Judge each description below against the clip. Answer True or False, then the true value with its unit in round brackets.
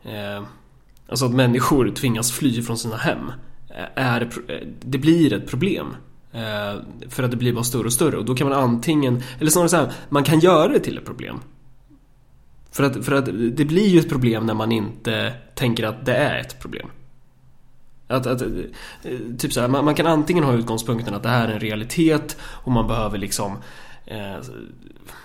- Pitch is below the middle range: True (125 Hz)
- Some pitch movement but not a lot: True (3.7 semitones)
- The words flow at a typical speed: True (185 wpm)